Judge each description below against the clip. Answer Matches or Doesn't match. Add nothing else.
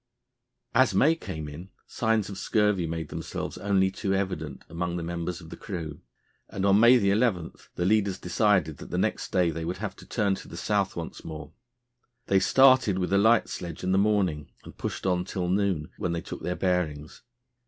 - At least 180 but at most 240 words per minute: Matches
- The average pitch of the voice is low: Matches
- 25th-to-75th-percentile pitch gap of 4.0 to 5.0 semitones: Doesn't match